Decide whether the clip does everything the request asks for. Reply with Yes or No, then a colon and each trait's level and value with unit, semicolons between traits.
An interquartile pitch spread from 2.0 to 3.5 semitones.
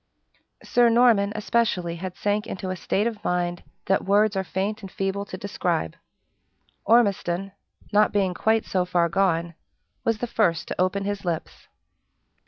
Yes: average, 2.9 semitones